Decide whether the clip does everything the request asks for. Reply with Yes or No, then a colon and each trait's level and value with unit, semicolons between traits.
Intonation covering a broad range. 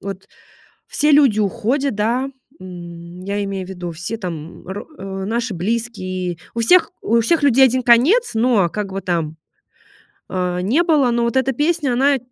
Yes: wide, 5.9 semitones